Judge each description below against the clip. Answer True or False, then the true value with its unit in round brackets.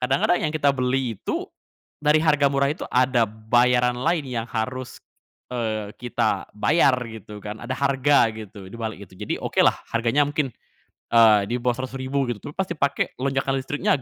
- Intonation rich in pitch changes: False (3.5 semitones)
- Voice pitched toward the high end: False (125 Hz)